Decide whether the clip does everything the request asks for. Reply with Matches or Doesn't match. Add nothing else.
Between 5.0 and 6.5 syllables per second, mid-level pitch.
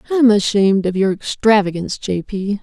Doesn't match